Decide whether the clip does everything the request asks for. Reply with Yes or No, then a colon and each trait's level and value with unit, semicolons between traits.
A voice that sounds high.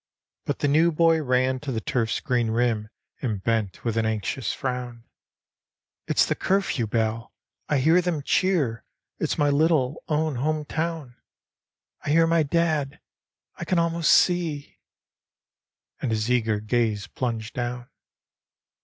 No: low, 130 Hz